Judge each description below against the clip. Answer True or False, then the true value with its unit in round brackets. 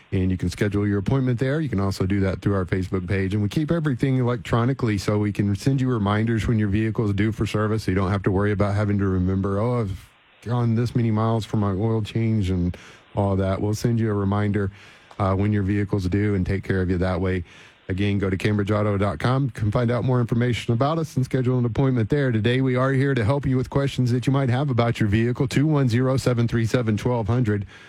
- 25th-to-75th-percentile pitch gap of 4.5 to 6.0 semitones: False (3.7 semitones)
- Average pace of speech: False (250 wpm)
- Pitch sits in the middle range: False (110 Hz)